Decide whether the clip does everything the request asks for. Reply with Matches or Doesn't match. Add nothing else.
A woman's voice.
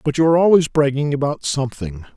Doesn't match